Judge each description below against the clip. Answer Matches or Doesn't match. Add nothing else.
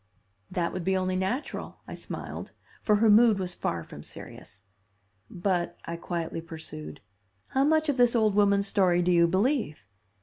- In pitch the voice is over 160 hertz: Matches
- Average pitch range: Matches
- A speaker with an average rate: Matches